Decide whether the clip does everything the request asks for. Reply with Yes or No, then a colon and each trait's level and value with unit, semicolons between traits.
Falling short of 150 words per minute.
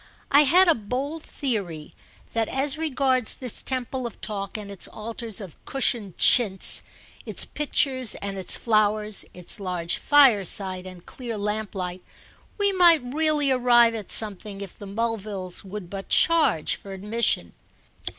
Yes: average, 140 wpm